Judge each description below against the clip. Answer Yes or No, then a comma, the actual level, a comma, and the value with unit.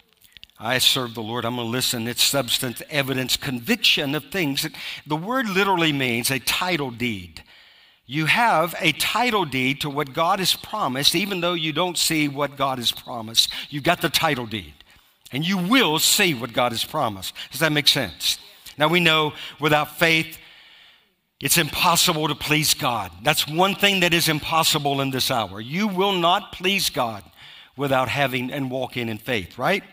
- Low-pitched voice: No, medium, 145 Hz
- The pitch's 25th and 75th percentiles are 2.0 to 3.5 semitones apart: No, average, 4.6 semitones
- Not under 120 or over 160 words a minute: No, average, 175 wpm